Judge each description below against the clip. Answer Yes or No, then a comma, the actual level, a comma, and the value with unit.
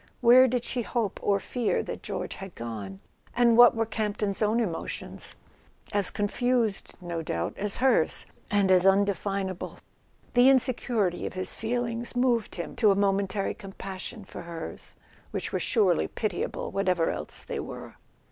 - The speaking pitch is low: No, high, 205 Hz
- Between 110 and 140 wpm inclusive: No, average, 150 wpm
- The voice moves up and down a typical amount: Yes, average, 3.9 semitones